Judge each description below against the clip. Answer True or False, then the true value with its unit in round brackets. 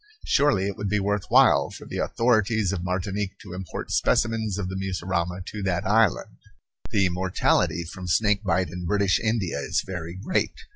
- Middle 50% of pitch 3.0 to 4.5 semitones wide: False (2.5 semitones)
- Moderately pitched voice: False (95 Hz)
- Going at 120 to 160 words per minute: False (175 wpm)